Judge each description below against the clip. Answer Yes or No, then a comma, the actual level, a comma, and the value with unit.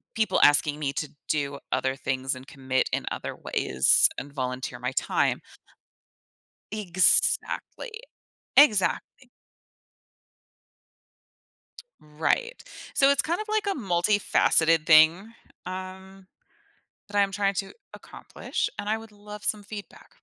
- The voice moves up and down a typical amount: No, wide, 6.3 semitones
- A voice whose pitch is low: No, high, 190 Hz